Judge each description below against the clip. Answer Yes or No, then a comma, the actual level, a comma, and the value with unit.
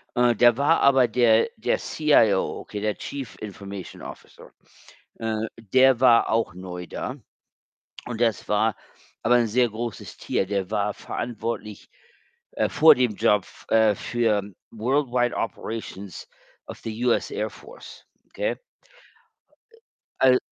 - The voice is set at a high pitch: No, low, 115 Hz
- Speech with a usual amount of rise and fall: Yes, average, 3.1 semitones